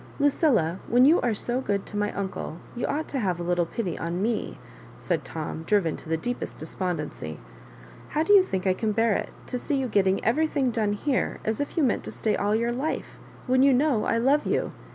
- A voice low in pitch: No, high, 225 Hz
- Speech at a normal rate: No, fast, 235 wpm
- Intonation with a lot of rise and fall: Yes, wide, 5.9 semitones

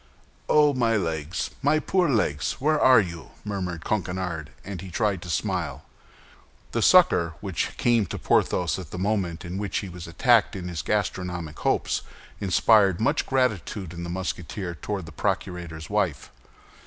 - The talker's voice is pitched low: Yes, very low, 95 Hz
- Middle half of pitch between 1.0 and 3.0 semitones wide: No, average, 4.0 semitones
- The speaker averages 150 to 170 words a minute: Yes, average, 155 wpm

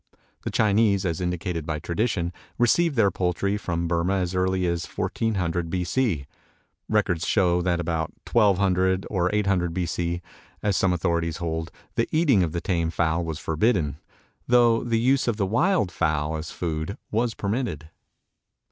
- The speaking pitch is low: Yes, very low, 90 Hz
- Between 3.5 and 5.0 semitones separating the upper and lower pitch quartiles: Yes, average, 3.9 semitones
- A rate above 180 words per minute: No, average, 155 wpm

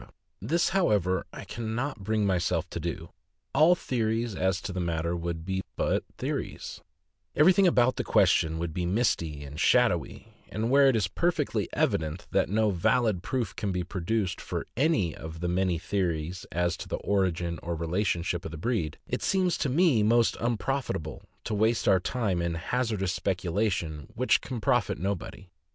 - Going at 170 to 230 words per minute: Yes, average, 175 wpm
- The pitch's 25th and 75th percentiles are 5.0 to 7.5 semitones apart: Yes, wide, 5.5 semitones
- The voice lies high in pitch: No, very low, 95 Hz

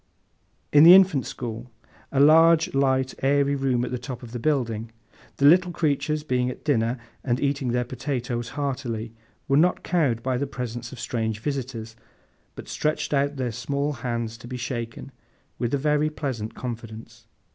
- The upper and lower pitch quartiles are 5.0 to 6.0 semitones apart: No, average, 3.4 semitones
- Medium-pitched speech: No, low, 130 Hz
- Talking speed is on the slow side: No, average, 160 wpm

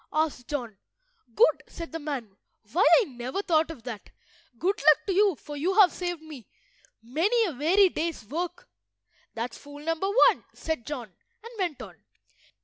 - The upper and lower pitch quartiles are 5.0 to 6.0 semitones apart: Yes, average, 5.3 semitones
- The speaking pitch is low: No, very high, 315 Hz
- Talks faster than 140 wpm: Yes, average, 165 wpm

